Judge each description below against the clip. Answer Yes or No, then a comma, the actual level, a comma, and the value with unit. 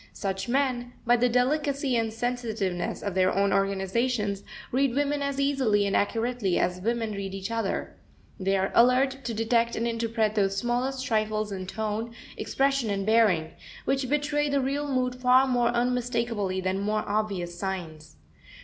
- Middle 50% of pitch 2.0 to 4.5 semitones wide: Yes, average, 4.1 semitones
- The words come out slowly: No, average, 160 wpm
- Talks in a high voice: Yes, high, 230 Hz